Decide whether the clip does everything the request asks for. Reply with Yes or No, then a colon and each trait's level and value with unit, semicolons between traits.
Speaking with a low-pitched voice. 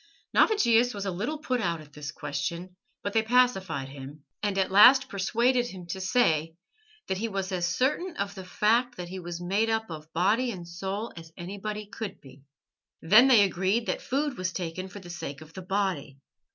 No: high, 190 Hz